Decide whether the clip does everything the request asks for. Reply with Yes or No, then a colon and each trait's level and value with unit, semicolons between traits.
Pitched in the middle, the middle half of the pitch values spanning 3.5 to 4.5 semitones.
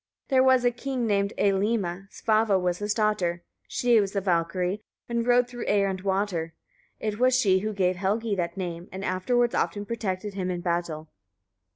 No: high, 200 Hz; average, 3.9 semitones